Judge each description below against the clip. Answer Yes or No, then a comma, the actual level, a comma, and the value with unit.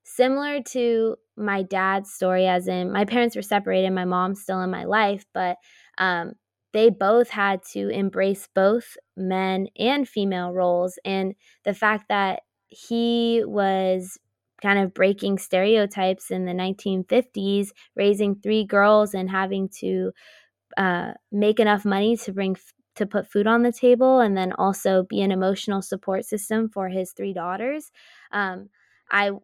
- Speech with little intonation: Yes, narrow, 2.3 semitones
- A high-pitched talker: Yes, high, 200 Hz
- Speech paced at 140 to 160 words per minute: Yes, average, 155 wpm